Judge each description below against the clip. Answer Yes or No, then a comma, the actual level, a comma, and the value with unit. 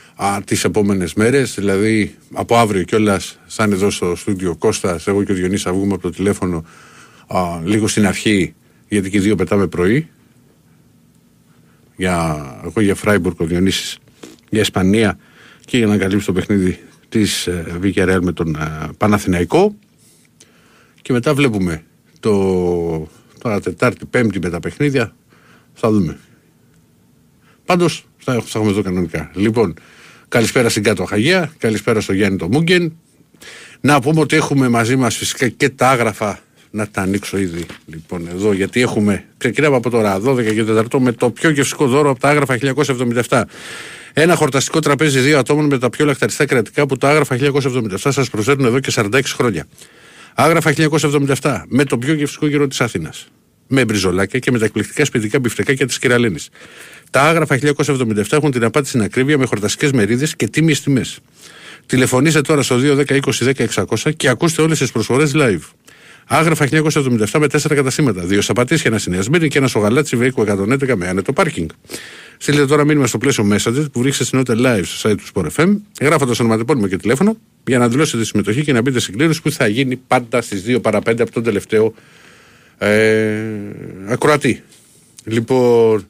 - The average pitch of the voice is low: Yes, low, 120 Hz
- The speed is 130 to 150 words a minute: No, average, 165 wpm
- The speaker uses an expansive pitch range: Yes, wide, 5.9 semitones